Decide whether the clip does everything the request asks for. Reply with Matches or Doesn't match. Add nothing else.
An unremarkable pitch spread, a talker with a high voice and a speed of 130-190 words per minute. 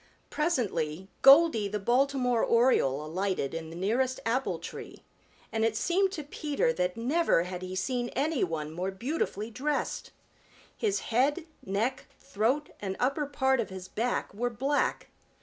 Doesn't match